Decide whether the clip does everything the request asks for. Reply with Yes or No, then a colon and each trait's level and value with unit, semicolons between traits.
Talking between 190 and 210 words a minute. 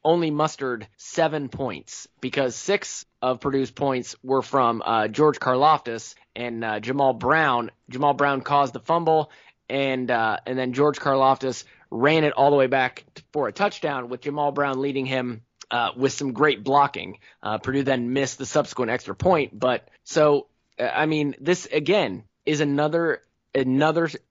No: average, 160 wpm